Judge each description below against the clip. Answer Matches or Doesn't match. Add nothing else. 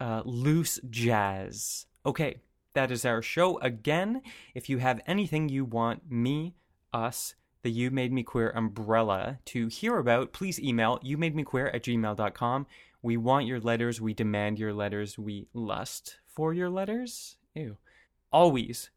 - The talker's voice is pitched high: Doesn't match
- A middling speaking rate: Matches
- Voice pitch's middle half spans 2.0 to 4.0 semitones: Doesn't match